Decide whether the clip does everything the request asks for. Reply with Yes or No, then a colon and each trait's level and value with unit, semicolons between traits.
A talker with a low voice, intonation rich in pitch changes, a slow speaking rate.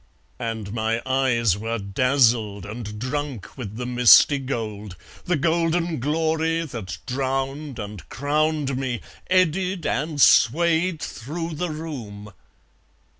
Yes: low, 130 Hz; wide, 5.8 semitones; slow, 115 wpm